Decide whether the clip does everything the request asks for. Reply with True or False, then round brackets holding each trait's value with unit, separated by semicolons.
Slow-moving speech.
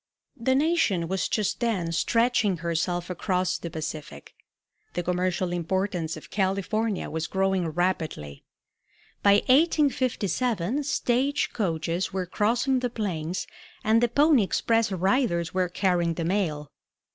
True (125 wpm)